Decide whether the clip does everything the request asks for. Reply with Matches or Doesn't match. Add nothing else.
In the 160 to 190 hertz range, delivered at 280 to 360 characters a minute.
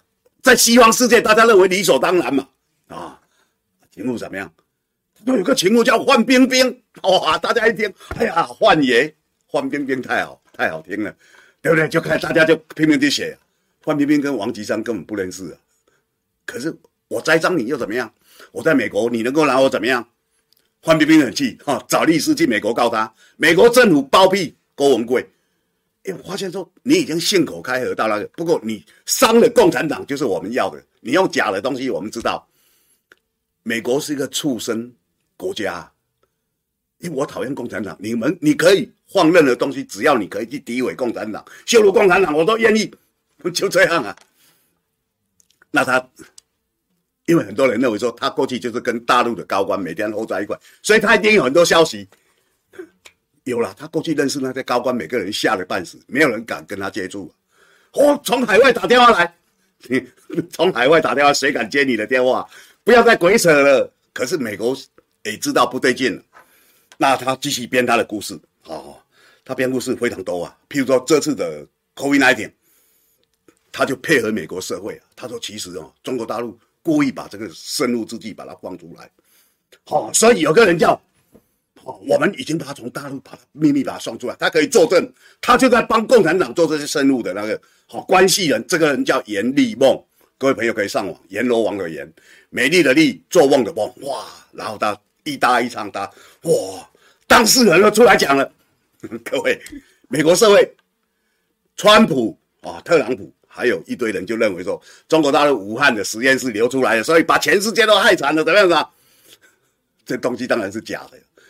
Matches